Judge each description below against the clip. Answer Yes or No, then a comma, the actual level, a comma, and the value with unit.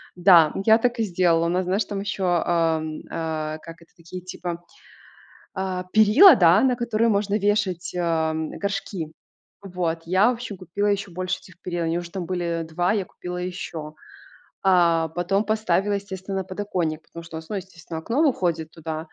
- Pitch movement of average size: Yes, average, 3.3 semitones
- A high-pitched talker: No, medium, 180 Hz